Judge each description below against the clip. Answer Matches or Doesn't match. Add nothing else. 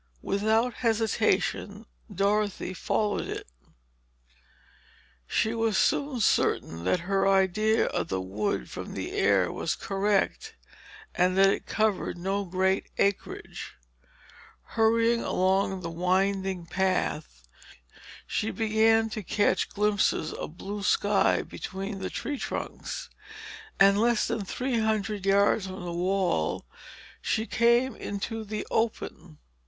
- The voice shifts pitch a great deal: Doesn't match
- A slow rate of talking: Matches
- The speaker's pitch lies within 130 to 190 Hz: Doesn't match